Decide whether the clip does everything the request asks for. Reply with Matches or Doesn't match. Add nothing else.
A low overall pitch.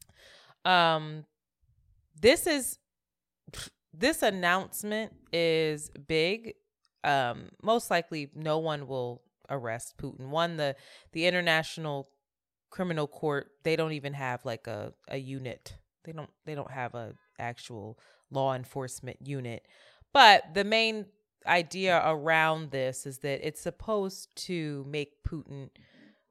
Doesn't match